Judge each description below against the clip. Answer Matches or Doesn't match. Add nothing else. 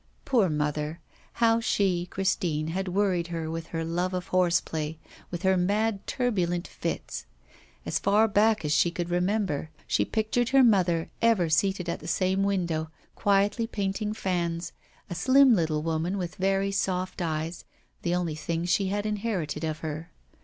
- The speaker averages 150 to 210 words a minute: Matches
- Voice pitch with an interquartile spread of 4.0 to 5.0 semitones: Doesn't match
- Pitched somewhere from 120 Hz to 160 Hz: Doesn't match